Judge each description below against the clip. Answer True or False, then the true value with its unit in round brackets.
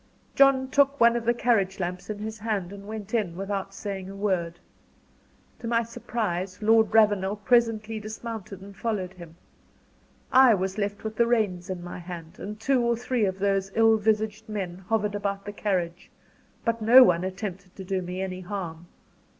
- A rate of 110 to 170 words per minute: False (180 wpm)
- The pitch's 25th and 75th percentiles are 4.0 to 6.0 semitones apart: False (3.1 semitones)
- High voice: True (205 Hz)